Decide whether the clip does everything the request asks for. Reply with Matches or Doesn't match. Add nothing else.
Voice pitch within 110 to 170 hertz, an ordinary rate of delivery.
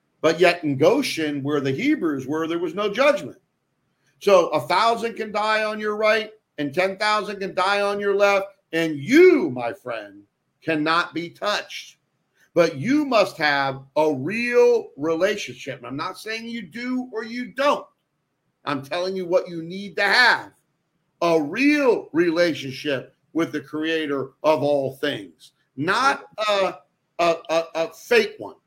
Doesn't match